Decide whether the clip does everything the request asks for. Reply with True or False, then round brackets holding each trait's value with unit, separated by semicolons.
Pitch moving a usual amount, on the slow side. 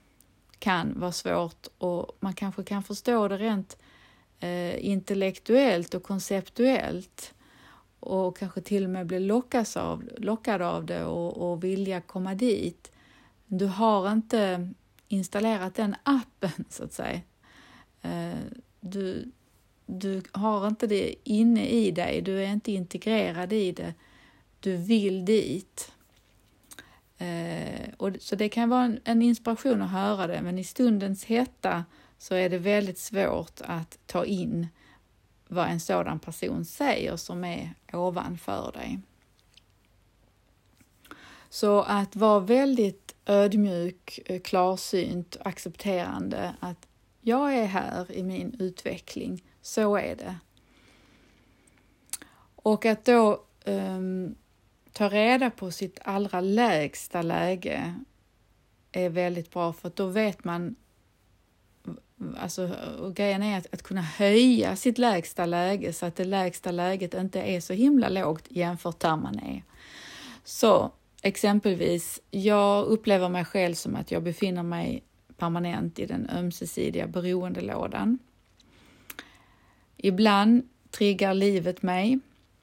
True (3.3 semitones; 120 wpm)